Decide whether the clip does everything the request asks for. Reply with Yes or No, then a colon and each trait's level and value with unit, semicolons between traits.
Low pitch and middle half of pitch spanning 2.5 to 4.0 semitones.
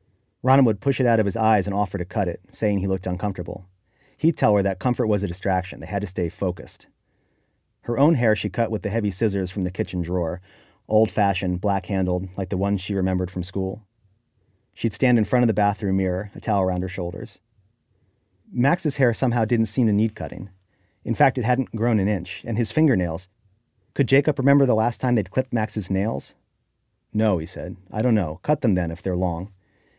Yes: low, 105 Hz; average, 3.6 semitones